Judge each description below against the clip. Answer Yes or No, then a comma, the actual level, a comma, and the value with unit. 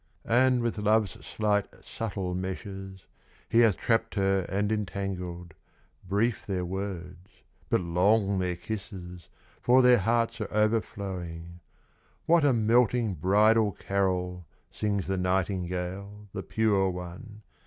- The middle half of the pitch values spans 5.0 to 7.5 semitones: No, average, 3.2 semitones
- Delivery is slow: Yes, slow, 120 wpm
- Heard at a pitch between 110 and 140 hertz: No, low, 100 Hz